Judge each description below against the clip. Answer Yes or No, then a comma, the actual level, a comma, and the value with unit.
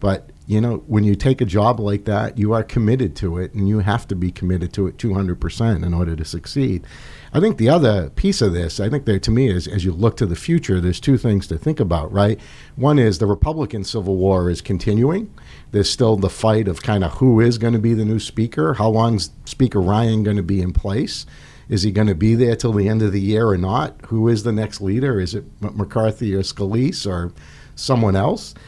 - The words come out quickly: Yes, fast, 230 wpm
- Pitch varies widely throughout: No, average, 3.2 semitones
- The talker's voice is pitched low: Yes, low, 105 Hz